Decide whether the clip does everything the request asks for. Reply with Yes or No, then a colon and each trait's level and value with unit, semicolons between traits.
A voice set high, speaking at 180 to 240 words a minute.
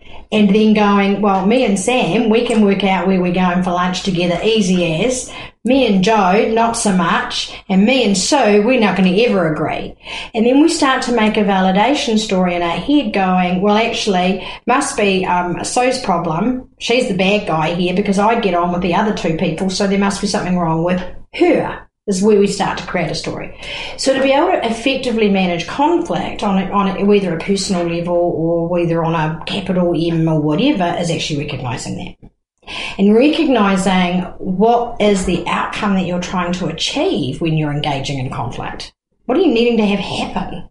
Yes: high, 195 Hz; average, 200 wpm